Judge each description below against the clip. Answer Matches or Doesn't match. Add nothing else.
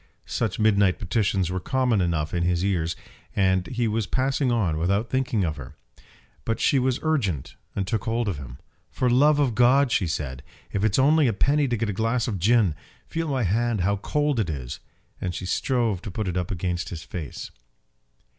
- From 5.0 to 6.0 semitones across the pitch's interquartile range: Matches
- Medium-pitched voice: Doesn't match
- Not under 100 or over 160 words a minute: Doesn't match